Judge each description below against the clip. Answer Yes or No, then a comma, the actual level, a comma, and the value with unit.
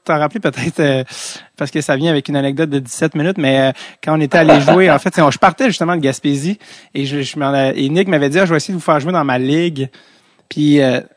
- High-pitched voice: No, medium, 150 Hz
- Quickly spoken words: Yes, fast, 265 wpm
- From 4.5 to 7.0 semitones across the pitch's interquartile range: No, average, 3.7 semitones